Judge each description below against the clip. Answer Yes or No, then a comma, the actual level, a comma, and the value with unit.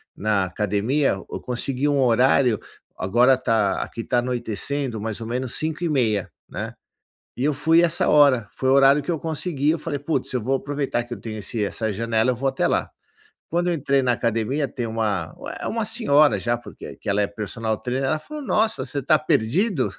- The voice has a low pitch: Yes, low, 130 Hz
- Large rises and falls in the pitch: No, average, 4.6 semitones